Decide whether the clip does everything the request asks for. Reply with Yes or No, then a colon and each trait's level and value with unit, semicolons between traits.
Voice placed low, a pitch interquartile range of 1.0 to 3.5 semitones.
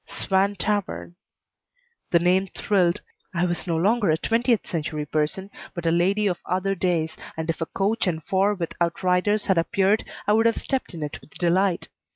No: medium, 185 Hz; average, 3.1 semitones